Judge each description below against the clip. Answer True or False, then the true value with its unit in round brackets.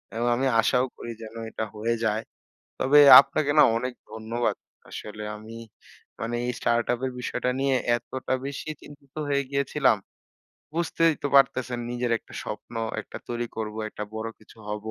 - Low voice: True (120 Hz)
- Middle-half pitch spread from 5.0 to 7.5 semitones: False (3.5 semitones)